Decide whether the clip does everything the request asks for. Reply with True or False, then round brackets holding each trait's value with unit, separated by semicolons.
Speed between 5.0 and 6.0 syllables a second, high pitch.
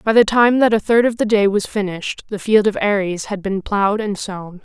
True (5.2 syllables/s; 205 Hz)